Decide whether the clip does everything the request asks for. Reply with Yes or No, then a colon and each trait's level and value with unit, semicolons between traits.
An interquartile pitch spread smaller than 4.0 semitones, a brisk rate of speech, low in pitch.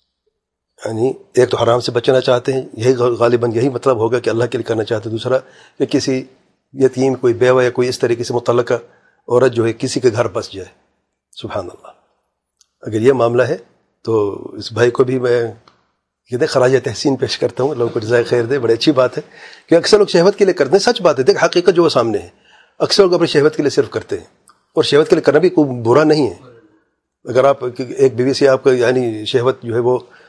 No: average, 4.6 semitones; fast, 230 wpm; low, 130 Hz